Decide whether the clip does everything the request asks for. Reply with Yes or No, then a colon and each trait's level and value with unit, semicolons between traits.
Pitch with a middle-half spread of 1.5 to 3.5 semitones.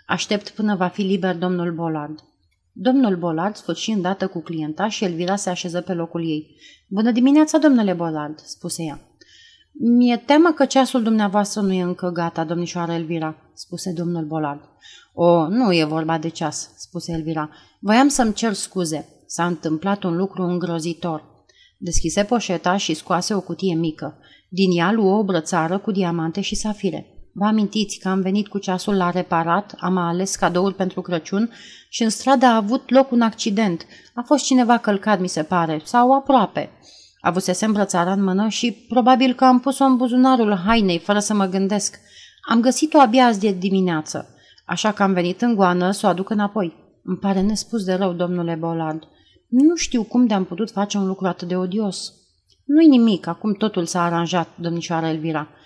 No: average, 4.3 semitones